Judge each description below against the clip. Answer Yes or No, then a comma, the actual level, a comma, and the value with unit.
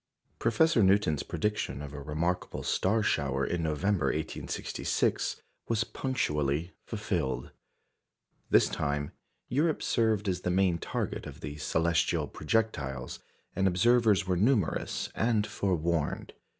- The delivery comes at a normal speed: No, slow, 115 wpm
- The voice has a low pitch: Yes, very low, 90 Hz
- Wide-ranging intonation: Yes, wide, 6.0 semitones